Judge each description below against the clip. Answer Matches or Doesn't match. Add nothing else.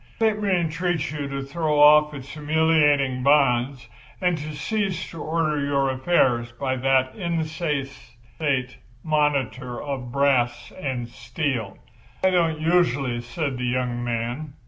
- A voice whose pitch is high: Doesn't match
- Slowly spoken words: Matches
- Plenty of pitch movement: Doesn't match